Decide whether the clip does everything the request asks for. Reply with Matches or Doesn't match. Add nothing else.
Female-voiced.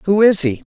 Doesn't match